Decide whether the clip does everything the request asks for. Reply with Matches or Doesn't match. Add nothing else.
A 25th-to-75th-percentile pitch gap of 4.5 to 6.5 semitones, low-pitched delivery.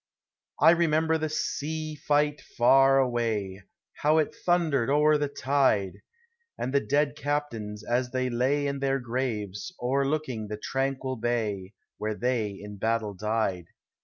Matches